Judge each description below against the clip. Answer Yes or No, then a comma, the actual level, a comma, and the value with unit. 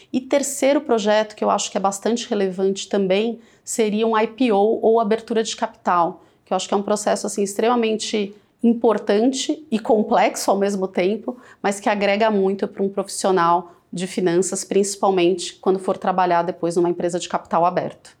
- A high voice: Yes, high, 205 Hz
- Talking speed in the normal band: Yes, average, 170 wpm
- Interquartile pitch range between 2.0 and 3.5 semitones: Yes, average, 2.9 semitones